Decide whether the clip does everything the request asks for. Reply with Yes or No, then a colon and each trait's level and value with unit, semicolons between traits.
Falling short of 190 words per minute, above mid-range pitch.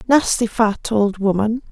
Yes: average, 140 wpm; high, 220 Hz